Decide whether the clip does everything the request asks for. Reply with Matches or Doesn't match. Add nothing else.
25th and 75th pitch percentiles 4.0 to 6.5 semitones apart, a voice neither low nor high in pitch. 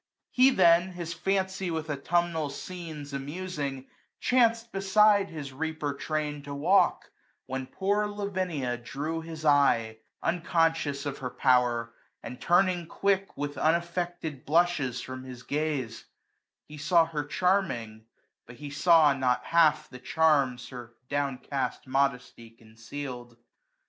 Matches